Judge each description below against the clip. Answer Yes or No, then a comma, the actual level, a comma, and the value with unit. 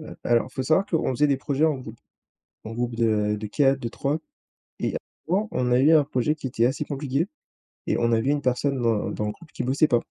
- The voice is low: Yes, low, 130 Hz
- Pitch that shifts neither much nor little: Yes, average, 4.0 semitones